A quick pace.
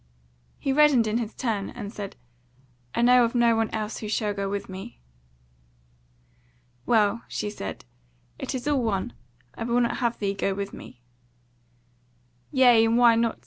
No: average, 165 wpm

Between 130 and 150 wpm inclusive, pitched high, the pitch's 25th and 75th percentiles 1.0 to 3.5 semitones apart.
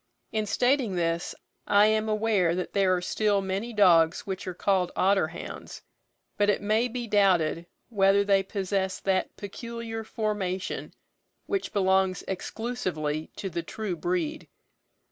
Yes: average, 140 wpm; high, 195 Hz; average, 2.9 semitones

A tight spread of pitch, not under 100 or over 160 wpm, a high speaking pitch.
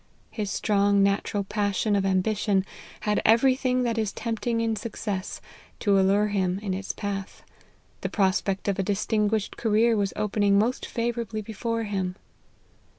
Yes: narrow, 2.2 semitones; average, 150 wpm; high, 205 Hz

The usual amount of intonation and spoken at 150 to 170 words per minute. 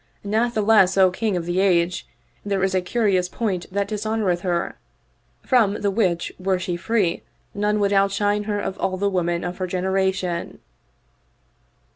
No: narrow, 2.3 semitones; average, 155 wpm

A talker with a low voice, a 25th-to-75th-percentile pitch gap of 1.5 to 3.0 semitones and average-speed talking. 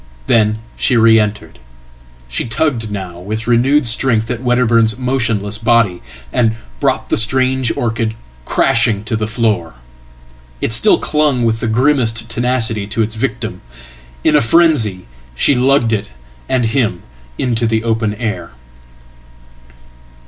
No: low, 115 Hz; narrow, 2.4 semitones; slow, 125 wpm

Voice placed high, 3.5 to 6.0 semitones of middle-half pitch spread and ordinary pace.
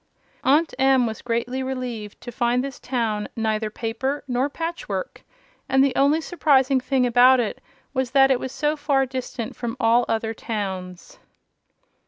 No: very high, 255 Hz; average, 2.9 semitones; average, 160 wpm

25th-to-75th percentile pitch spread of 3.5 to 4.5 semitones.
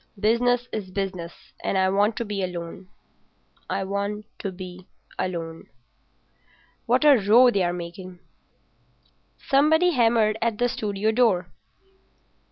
Yes: average, 4.1 semitones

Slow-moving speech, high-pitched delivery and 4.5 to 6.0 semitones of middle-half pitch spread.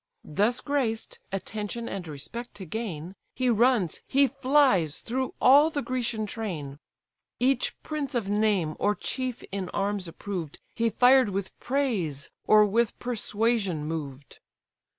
Yes: slow, 130 wpm; high, 215 Hz; average, 5.3 semitones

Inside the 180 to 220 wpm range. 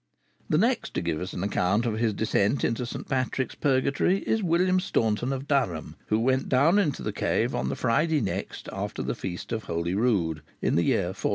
Yes: average, 200 wpm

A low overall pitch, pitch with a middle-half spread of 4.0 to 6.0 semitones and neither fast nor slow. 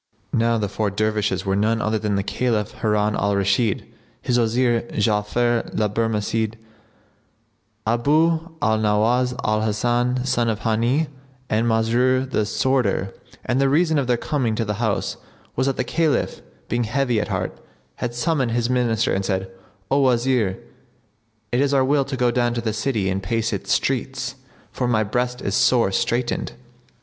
No: low, 115 Hz; average, 2.8 semitones; average, 165 wpm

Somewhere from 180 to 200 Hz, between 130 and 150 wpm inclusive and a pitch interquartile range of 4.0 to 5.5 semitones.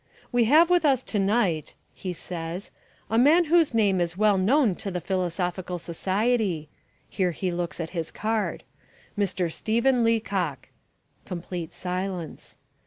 Yes: high, 190 Hz; average, 140 wpm; average, 4.6 semitones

